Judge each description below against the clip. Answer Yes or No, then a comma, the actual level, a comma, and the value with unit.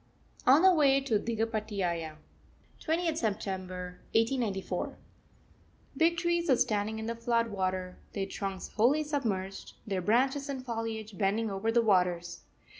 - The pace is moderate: No, slow, 130 wpm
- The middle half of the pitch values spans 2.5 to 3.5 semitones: No, wide, 5.4 semitones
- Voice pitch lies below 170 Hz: No, high, 220 Hz